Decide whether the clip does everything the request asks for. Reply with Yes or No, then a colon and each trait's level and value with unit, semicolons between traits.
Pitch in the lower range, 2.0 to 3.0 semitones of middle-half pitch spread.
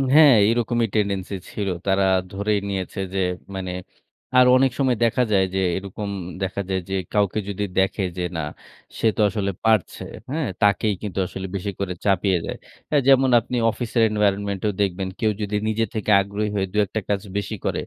Yes: low, 100 Hz; narrow, 2.4 semitones